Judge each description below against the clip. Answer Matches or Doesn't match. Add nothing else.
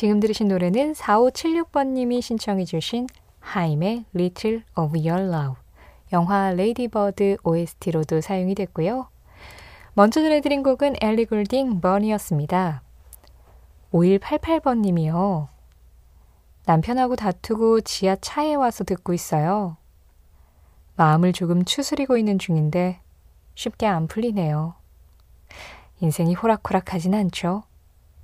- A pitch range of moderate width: Doesn't match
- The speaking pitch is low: Doesn't match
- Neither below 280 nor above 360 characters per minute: Doesn't match